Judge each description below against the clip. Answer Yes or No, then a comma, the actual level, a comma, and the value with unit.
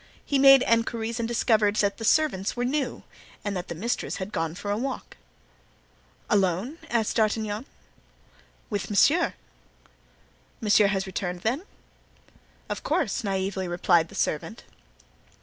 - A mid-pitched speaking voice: No, high, 210 Hz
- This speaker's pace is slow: Yes, slow, 130 wpm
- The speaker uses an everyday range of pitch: Yes, average, 3.8 semitones